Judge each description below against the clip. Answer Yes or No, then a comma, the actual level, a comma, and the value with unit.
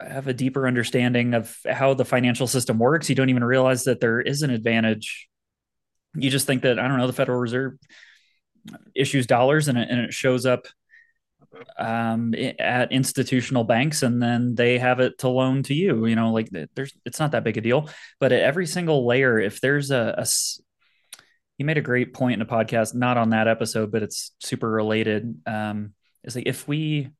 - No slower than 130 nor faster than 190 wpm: No, average, 200 wpm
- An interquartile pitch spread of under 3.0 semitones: Yes, narrow, 2.6 semitones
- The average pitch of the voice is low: Yes, low, 125 Hz